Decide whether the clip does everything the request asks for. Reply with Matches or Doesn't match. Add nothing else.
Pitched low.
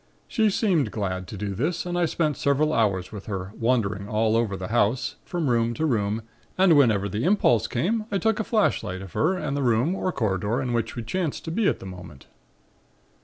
Matches